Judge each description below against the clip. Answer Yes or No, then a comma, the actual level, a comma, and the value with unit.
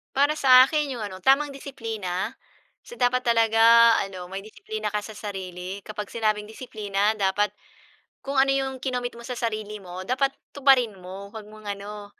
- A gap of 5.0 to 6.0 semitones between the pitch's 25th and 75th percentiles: No, average, 4.0 semitones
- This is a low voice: No, high, 220 Hz